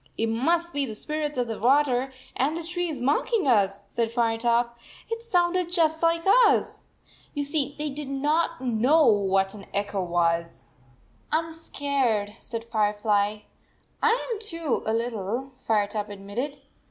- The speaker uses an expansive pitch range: Yes, wide, 6.7 semitones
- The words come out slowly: No, average, 150 wpm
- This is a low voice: No, very high, 250 Hz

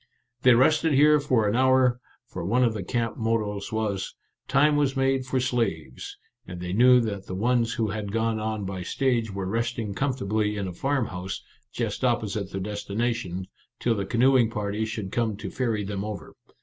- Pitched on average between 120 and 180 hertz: No, low, 110 Hz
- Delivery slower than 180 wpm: No, average, 185 wpm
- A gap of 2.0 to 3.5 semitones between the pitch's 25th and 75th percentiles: No, average, 3.9 semitones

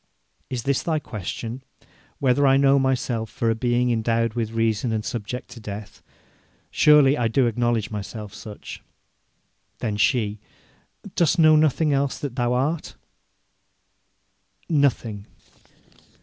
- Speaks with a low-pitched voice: Yes, low, 120 Hz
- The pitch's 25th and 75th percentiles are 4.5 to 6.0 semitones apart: No, average, 3.7 semitones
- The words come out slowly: Yes, slow, 125 wpm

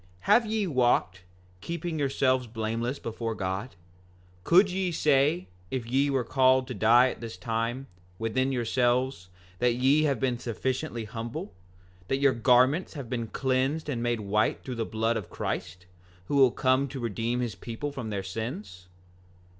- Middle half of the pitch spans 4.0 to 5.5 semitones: No, average, 3.2 semitones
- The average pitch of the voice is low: Yes, low, 125 Hz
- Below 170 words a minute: Yes, average, 160 wpm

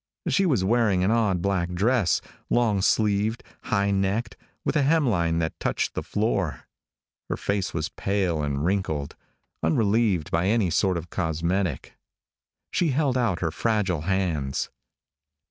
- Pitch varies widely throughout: No, average, 4.7 semitones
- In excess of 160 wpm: No, average, 140 wpm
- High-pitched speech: No, very low, 95 Hz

